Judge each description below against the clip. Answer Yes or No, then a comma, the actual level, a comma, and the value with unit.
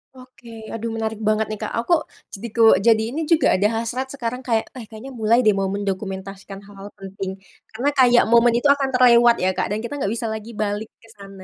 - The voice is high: Yes, high, 225 Hz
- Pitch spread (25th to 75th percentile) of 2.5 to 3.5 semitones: Yes, average, 3.1 semitones